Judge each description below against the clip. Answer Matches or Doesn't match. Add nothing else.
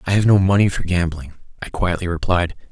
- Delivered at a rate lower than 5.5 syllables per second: Doesn't match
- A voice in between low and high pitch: Doesn't match